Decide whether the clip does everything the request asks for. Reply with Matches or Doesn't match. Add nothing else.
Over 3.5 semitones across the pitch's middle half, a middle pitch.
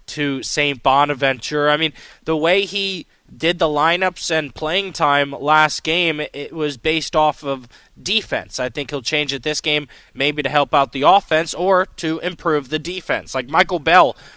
Doesn't match